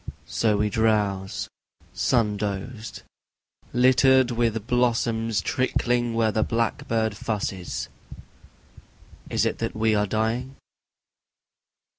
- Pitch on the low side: Yes, low, 110 Hz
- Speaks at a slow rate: Yes, slow, 95 wpm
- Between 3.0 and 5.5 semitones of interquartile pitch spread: No, narrow, 2.4 semitones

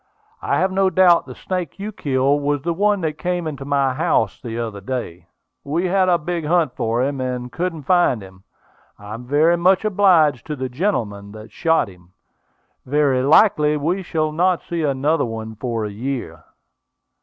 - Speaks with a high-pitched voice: No, medium, 145 Hz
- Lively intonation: Yes, wide, 6.3 semitones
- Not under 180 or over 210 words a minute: Yes, average, 185 wpm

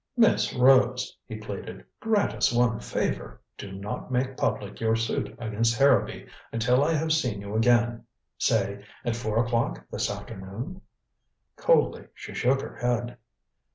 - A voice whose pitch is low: Yes, low, 120 Hz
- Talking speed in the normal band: Yes, average, 145 wpm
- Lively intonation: No, average, 2.8 semitones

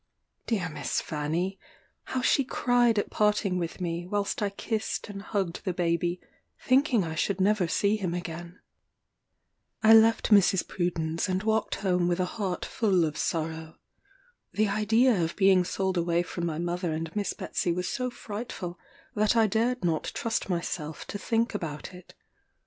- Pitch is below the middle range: No, medium, 185 Hz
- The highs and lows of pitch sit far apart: No, average, 3.9 semitones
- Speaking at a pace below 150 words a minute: No, average, 165 wpm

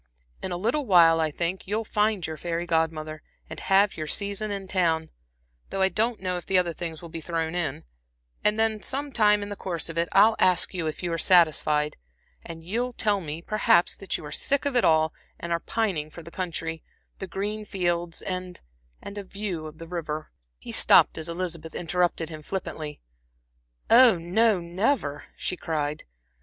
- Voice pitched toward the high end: No, medium, 175 Hz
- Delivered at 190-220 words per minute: Yes, average, 195 wpm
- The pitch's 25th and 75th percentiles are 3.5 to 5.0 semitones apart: Yes, average, 3.9 semitones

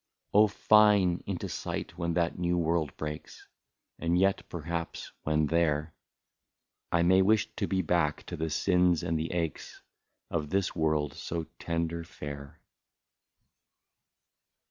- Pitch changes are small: Yes, narrow, 2.3 semitones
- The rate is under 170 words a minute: Yes, slow, 135 wpm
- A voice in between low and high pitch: No, very low, 85 Hz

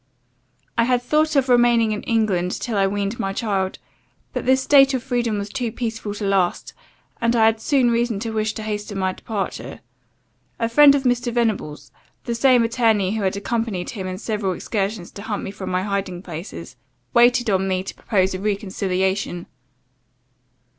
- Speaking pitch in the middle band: No, high, 215 Hz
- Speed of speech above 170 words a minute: Yes, average, 180 wpm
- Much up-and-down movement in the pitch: No, average, 3.6 semitones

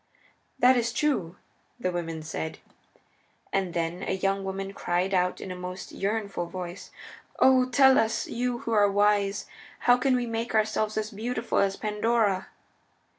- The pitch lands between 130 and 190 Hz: No, high, 205 Hz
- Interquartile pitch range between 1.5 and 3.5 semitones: No, average, 4.0 semitones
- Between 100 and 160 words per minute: Yes, average, 155 wpm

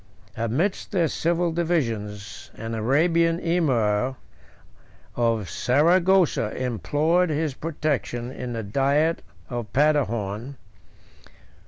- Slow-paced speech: Yes, slow, 85 wpm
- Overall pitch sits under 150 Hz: Yes, medium, 140 Hz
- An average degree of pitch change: No, wide, 6.3 semitones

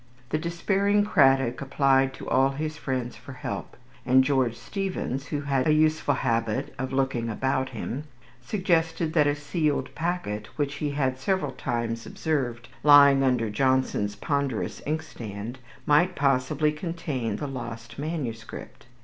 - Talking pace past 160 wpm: No, average, 140 wpm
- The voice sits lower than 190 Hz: Yes, low, 135 Hz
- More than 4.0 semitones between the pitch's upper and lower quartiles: No, average, 3.7 semitones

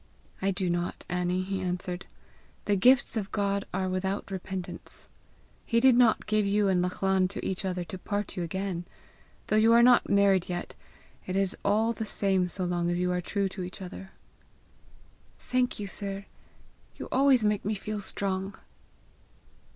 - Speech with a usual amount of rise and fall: No, narrow, 2.3 semitones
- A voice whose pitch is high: Yes, high, 195 Hz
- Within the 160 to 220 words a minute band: Yes, average, 170 wpm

